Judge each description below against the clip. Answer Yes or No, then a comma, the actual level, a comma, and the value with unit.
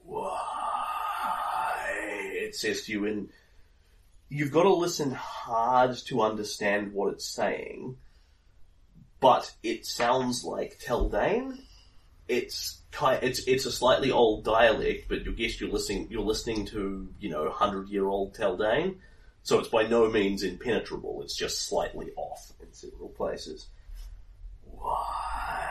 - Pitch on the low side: Yes, low, 115 Hz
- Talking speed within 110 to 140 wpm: Yes, slow, 135 wpm